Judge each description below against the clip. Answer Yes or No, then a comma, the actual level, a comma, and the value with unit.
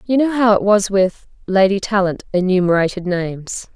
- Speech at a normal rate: Yes, average, 160 wpm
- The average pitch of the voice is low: No, high, 195 Hz